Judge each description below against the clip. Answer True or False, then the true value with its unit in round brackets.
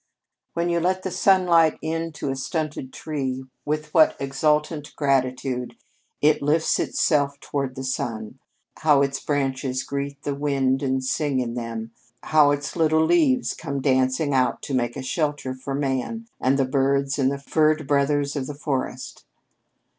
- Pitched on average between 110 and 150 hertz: True (140 Hz)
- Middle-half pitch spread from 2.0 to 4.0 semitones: True (2.6 semitones)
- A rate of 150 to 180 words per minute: True (160 wpm)